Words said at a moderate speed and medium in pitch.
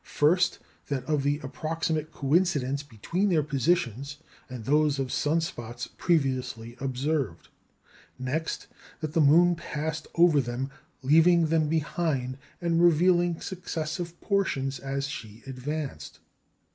No: slow, 120 wpm; medium, 150 Hz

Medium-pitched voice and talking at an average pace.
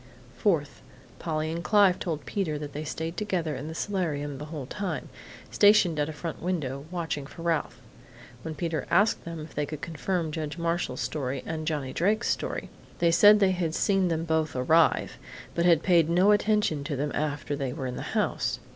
Yes: medium, 160 Hz; average, 190 wpm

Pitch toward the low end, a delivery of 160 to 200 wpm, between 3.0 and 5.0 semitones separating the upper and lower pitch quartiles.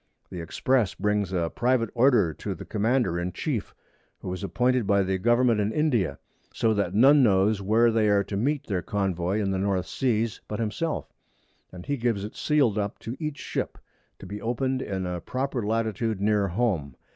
Yes: low, 105 Hz; average, 190 wpm; average, 4.0 semitones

